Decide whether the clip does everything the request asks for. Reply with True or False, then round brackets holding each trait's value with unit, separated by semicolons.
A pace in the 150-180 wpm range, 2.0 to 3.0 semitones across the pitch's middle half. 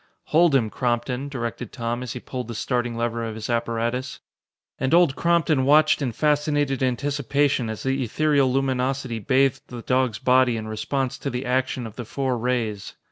True (175 wpm; 2.7 semitones)